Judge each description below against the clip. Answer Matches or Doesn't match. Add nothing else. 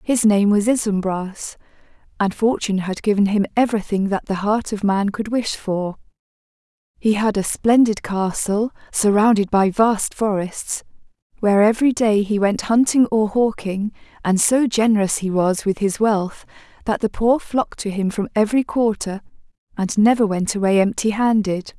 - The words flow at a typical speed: Matches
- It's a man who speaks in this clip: Doesn't match